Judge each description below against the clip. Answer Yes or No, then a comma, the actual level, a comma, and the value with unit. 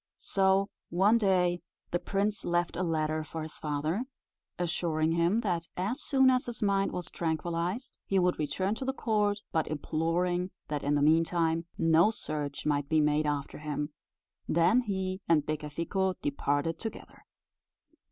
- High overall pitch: No, medium, 170 Hz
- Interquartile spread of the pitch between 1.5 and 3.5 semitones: No, average, 4.0 semitones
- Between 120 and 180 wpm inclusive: Yes, average, 150 wpm